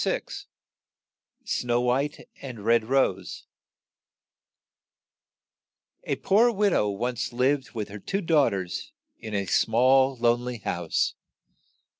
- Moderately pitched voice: No, low, 125 Hz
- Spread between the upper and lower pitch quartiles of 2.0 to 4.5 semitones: Yes, average, 3.5 semitones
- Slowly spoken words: Yes, slow, 115 wpm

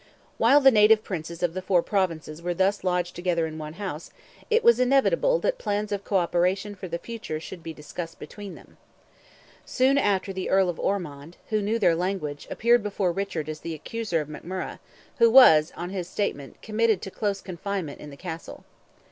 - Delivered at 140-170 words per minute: No, average, 190 wpm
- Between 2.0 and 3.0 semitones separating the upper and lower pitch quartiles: No, average, 3.9 semitones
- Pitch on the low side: No, medium, 185 Hz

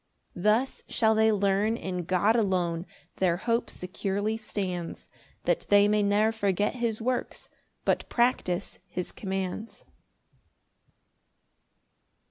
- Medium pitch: No, high, 205 Hz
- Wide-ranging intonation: No, average, 3.0 semitones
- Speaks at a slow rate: Yes, slow, 110 wpm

